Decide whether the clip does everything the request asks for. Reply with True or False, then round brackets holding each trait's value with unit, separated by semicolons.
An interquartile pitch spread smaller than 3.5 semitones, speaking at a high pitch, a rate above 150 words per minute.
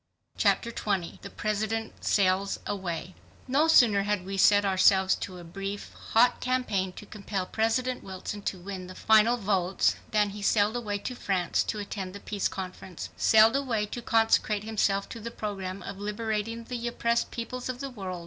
True (2.9 semitones; 205 Hz; 175 wpm)